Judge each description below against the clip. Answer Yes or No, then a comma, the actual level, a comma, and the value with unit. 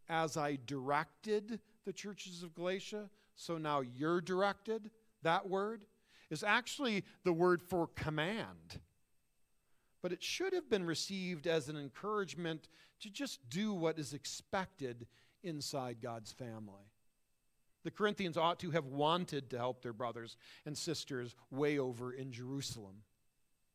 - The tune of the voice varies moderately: No, wide, 6.8 semitones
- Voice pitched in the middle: Yes, medium, 160 Hz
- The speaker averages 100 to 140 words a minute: Yes, slow, 135 wpm